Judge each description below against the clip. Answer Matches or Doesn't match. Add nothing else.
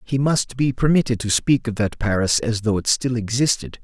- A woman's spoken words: Doesn't match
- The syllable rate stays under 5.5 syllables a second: Matches